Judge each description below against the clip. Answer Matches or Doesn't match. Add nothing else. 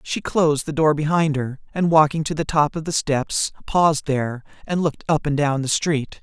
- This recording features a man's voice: Matches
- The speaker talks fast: Matches